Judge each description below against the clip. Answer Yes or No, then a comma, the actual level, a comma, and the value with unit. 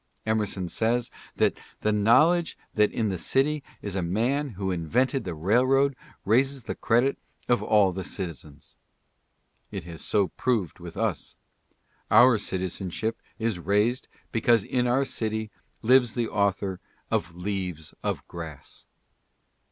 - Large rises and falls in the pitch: No, average, 4.7 semitones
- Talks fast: No, slow, 135 wpm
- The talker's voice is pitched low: Yes, low, 110 Hz